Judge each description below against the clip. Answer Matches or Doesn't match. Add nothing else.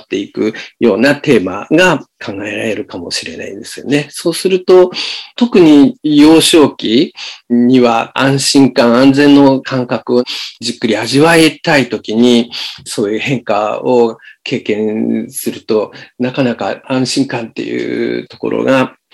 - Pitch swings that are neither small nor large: Doesn't match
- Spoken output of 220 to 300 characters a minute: Matches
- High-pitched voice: Doesn't match